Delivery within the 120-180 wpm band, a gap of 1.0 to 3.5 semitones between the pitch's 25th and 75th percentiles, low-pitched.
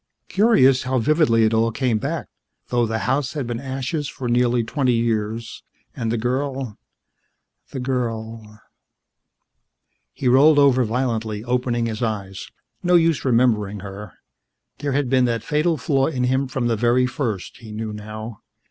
Yes: average, 155 wpm; average, 3.0 semitones; low, 120 Hz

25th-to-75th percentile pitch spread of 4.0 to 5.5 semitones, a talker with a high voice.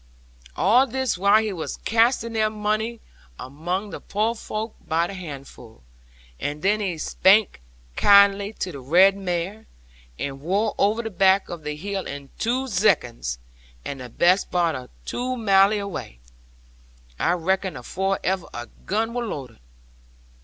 Yes: average, 4.7 semitones; high, 195 Hz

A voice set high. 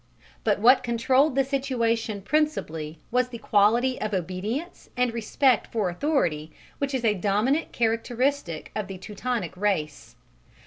Yes: high, 230 Hz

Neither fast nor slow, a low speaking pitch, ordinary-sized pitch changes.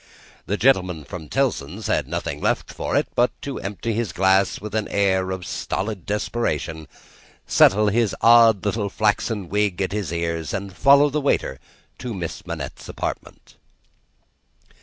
Yes: average, 150 wpm; low, 100 Hz; average, 3.5 semitones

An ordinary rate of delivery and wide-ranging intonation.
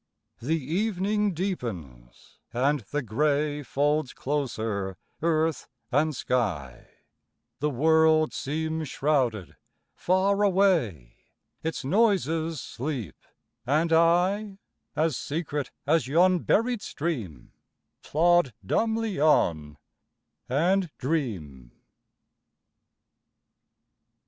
No: slow, 80 wpm; wide, 5.7 semitones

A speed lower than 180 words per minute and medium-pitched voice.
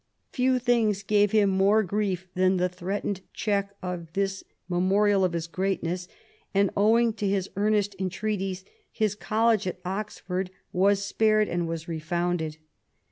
No: average, 140 wpm; high, 195 Hz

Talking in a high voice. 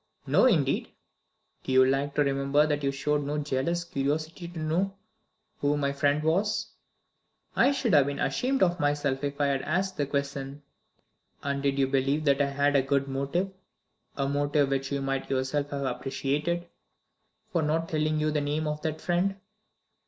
No: medium, 145 Hz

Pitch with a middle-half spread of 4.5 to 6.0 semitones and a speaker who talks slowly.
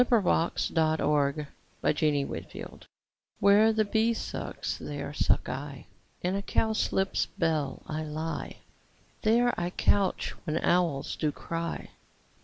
Yes: average, 5.1 semitones; slow, 110 wpm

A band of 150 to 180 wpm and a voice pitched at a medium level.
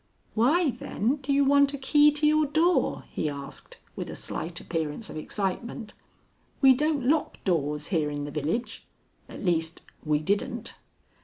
No: average, 160 wpm; high, 230 Hz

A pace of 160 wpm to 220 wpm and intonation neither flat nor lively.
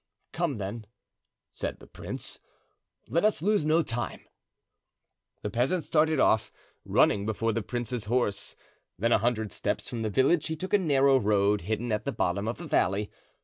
No: average, 170 wpm; wide, 6.5 semitones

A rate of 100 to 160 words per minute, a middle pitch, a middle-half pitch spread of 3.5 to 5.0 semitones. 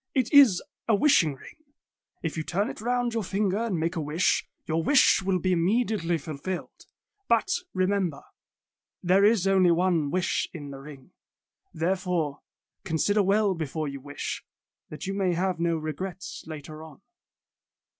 Yes: average, 155 wpm; medium, 180 Hz; average, 4.0 semitones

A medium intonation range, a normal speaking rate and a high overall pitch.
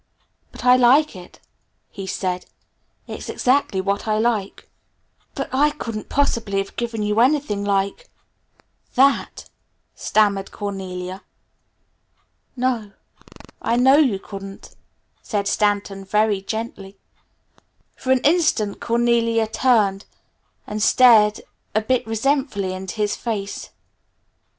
No: average, 3.8 semitones; slow, 110 wpm; high, 215 Hz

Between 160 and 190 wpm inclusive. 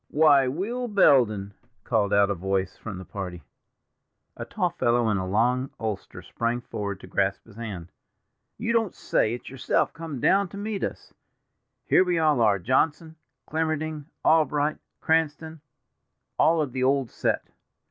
No: average, 150 wpm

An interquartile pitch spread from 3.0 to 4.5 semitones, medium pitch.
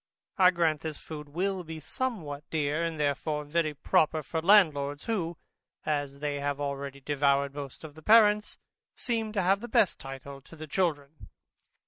Yes: average, 3.8 semitones; medium, 155 Hz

